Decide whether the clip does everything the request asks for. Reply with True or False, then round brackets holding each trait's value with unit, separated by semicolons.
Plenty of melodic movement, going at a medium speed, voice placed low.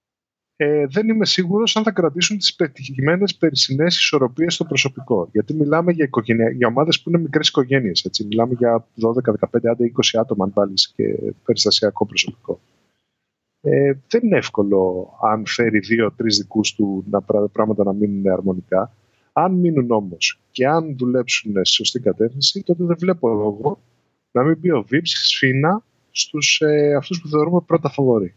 True (6.8 semitones; 160 wpm; 130 Hz)